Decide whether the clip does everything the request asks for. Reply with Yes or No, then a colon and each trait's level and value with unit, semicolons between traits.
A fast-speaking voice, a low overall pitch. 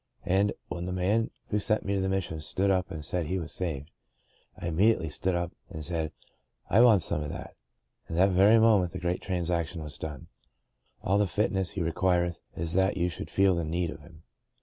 Yes: fast, 220 wpm; very low, 90 Hz